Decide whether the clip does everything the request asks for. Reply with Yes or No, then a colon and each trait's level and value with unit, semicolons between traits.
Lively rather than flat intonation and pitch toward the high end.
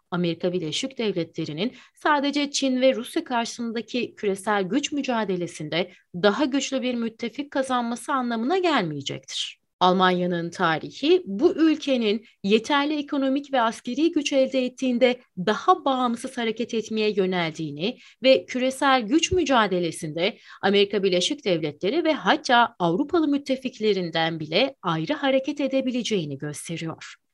Yes: wide, 6.8 semitones; high, 235 Hz